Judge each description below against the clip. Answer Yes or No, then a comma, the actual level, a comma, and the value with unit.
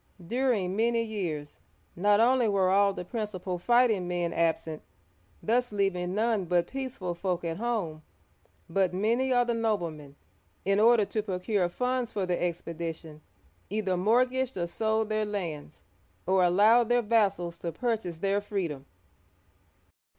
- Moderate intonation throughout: Yes, average, 4.6 semitones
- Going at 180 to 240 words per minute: No, average, 150 wpm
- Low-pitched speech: No, high, 200 Hz